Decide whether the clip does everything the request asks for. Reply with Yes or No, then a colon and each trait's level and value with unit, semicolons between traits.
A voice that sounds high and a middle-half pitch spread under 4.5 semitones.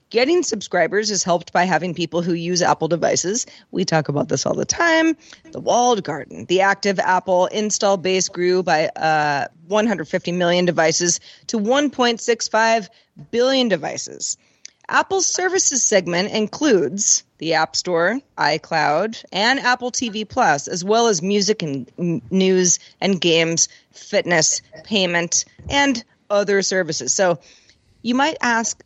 No: high, 195 Hz; average, 5.0 semitones